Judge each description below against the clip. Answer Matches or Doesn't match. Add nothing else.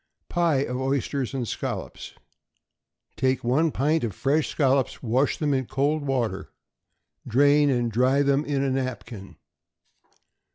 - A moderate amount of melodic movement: Doesn't match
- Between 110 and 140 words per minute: Matches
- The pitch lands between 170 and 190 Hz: Doesn't match